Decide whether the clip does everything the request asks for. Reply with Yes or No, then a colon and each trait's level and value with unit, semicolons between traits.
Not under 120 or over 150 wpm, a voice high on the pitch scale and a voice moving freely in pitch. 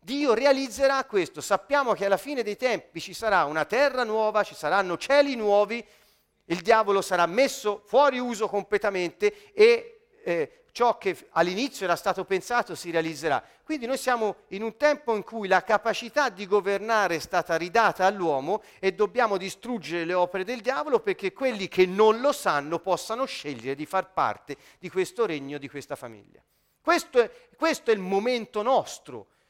No: average, 165 wpm; high, 210 Hz; wide, 5.9 semitones